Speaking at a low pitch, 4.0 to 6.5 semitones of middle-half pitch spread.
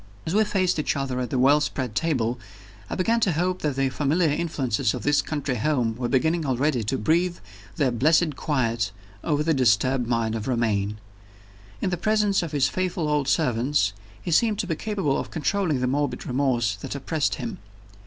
No: medium, 145 Hz; average, 5.1 semitones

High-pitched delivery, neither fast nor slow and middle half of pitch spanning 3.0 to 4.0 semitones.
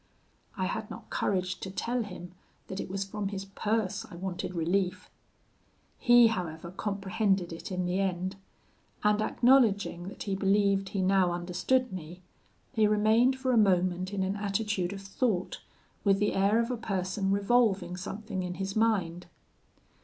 No: high, 195 Hz; average, 160 wpm; narrow, 2.5 semitones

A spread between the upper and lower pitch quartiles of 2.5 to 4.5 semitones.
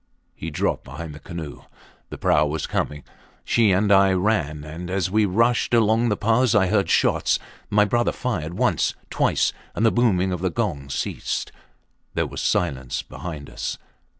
No: wide, 5.5 semitones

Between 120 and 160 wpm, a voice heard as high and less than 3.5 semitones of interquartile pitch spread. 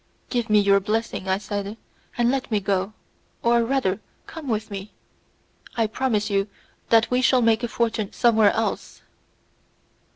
Yes: average, 155 wpm; high, 220 Hz; average, 2.8 semitones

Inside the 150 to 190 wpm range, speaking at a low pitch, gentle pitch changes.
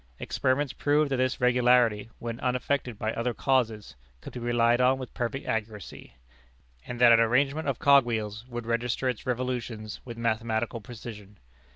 Yes: average, 160 wpm; low, 120 Hz; narrow, 2.1 semitones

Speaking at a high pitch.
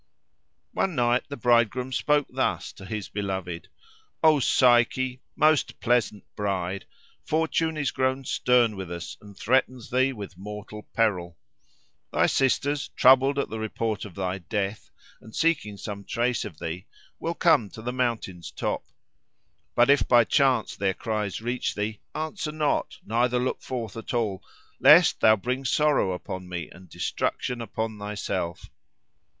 No: low, 115 Hz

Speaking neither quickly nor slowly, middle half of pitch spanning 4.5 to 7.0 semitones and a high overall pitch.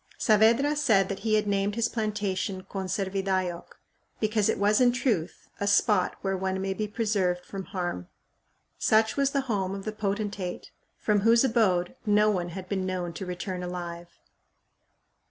No: average, 160 wpm; narrow, 2.5 semitones; high, 200 Hz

